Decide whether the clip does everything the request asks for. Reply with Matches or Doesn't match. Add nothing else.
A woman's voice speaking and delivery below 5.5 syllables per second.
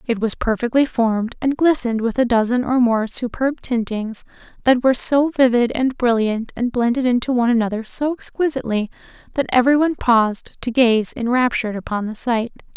Doesn't match